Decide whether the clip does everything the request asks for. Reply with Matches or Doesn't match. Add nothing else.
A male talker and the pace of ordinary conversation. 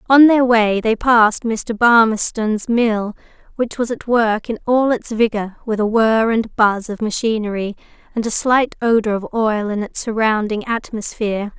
Doesn't match